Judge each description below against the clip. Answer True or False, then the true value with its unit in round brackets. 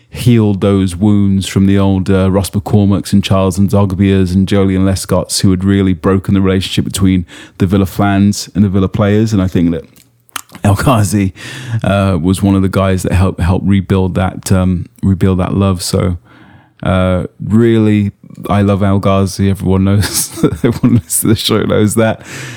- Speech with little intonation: True (1.4 semitones)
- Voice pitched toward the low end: True (100 Hz)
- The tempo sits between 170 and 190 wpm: True (180 wpm)